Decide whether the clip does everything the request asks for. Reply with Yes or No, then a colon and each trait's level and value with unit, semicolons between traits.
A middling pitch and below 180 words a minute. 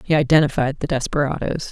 Yes: medium, 145 Hz; average, 140 wpm